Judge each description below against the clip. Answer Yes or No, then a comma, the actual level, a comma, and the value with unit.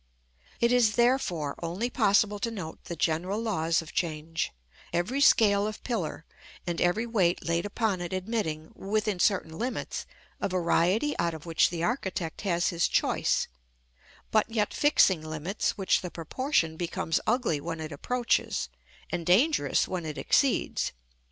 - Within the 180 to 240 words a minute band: No, average, 150 wpm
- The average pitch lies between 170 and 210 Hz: Yes, medium, 185 Hz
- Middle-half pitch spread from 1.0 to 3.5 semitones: No, average, 4.9 semitones